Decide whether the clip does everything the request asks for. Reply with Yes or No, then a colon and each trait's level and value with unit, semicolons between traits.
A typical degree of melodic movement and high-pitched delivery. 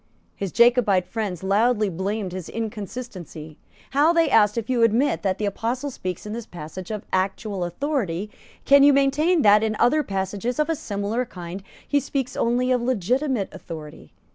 Yes: average, 4.9 semitones; high, 215 Hz